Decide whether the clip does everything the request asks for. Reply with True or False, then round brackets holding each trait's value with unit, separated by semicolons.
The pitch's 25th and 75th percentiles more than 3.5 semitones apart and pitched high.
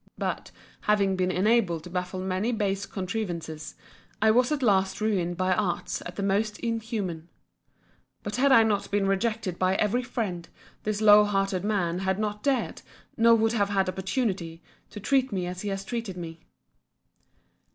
False (3.0 semitones; 200 Hz)